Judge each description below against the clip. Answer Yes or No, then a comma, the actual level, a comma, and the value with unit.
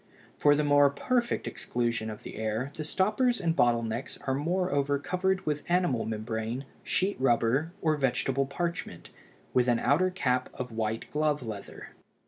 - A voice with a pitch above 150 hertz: No, medium, 140 Hz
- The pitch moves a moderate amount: No, wide, 6.1 semitones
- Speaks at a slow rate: No, average, 155 wpm